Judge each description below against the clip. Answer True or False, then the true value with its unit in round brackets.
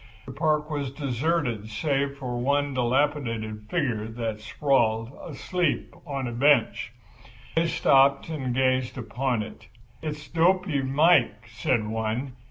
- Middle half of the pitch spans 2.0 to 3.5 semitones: False (4.2 semitones)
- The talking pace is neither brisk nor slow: False (125 wpm)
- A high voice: False (135 Hz)